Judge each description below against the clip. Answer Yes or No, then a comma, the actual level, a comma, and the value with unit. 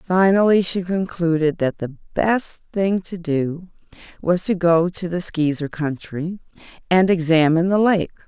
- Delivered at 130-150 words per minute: Yes, average, 145 wpm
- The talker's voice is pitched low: No, medium, 175 Hz